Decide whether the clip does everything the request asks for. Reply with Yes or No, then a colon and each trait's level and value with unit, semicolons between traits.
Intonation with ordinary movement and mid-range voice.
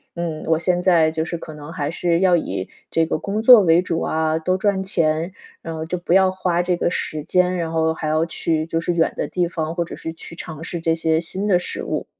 No: narrow, 2.0 semitones; medium, 165 Hz